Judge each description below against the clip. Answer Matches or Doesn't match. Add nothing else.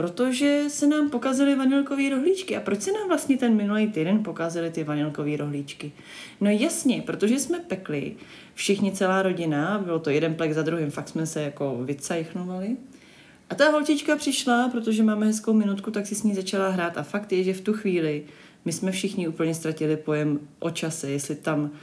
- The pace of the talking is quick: Matches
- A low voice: Doesn't match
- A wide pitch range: Matches